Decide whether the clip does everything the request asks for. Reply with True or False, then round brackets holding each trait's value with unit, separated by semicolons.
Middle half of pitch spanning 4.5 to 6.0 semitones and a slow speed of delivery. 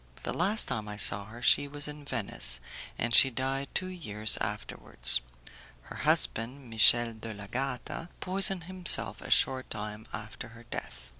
False (5.1 semitones; 155 wpm)